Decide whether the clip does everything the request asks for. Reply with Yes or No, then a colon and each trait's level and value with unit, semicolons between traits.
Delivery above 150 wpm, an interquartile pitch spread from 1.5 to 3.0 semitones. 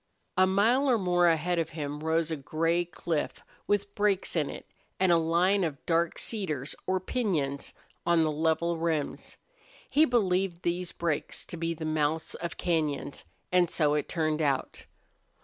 Yes: average, 165 wpm; average, 2.7 semitones